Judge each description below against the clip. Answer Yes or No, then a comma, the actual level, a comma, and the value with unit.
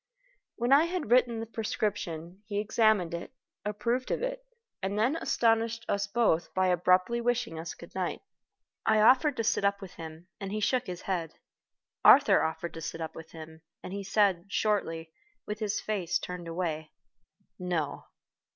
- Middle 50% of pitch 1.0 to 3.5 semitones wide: No, average, 5.0 semitones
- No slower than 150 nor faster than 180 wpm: Yes, average, 170 wpm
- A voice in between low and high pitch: No, high, 200 Hz